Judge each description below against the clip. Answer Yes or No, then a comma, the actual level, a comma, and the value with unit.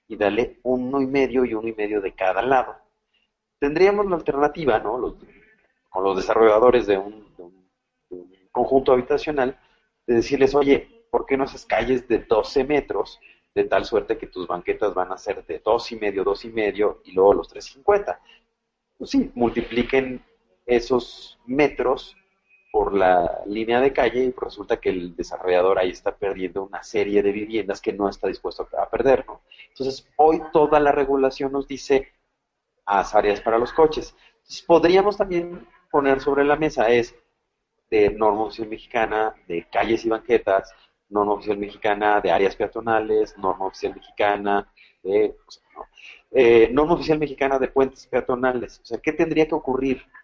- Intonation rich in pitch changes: Yes, wide, 7.1 semitones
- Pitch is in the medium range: No, low, 130 Hz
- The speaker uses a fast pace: No, average, 170 wpm